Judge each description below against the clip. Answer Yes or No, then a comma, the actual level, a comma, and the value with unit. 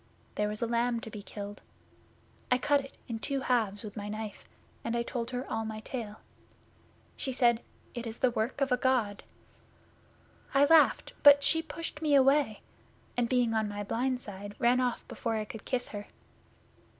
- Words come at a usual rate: Yes, average, 180 wpm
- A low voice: No, high, 235 Hz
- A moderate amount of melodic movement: Yes, average, 3.4 semitones